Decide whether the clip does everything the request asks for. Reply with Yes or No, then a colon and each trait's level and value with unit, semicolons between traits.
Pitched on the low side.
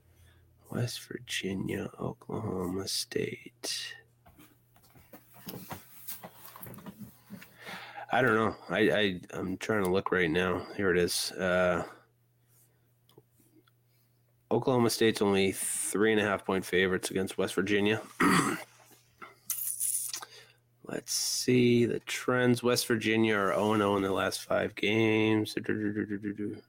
Yes: low, 110 Hz